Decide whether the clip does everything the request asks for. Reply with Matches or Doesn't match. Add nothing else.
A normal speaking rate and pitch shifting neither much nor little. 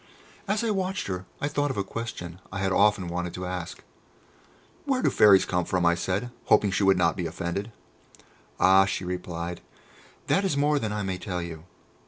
Matches